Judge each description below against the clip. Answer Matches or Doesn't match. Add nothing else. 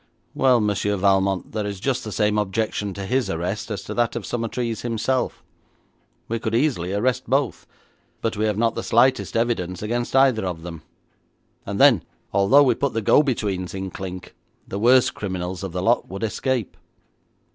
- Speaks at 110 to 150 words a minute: Doesn't match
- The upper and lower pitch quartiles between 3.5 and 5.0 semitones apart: Matches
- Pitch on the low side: Matches